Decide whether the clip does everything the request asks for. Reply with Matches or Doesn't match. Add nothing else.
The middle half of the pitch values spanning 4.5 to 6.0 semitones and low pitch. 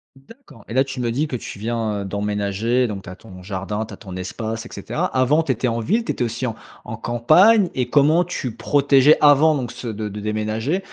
Matches